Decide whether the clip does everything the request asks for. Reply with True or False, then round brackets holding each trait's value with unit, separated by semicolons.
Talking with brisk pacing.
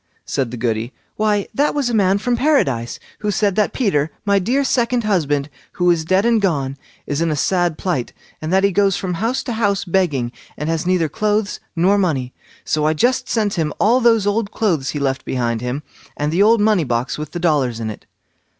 True (215 wpm)